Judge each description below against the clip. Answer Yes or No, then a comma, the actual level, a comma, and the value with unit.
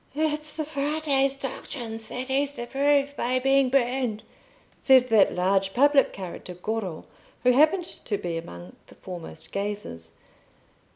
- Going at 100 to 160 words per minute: Yes, slow, 135 wpm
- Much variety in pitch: Yes, wide, 6.2 semitones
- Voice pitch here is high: Yes, very high, 250 Hz